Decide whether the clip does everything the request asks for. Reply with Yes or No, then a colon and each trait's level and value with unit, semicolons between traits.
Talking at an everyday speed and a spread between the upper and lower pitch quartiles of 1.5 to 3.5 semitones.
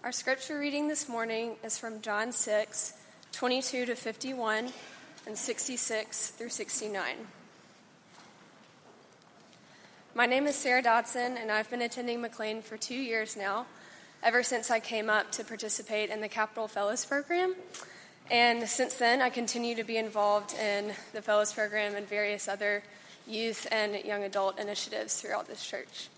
Yes: average, 150 wpm; narrow, 2.4 semitones